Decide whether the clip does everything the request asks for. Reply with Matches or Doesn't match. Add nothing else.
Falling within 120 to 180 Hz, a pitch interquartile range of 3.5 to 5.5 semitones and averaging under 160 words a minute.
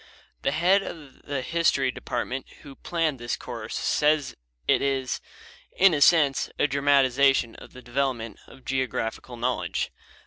Doesn't match